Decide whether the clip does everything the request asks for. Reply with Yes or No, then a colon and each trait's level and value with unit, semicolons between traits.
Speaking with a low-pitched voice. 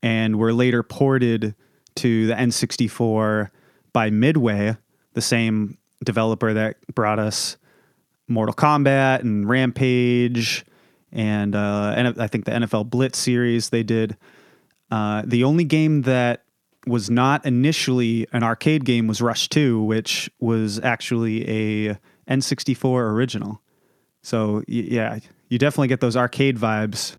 Yes: low, 115 Hz